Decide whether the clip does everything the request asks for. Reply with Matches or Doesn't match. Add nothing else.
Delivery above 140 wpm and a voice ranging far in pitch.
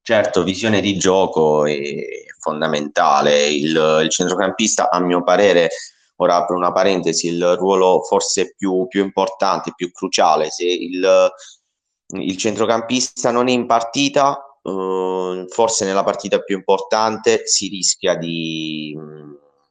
Doesn't match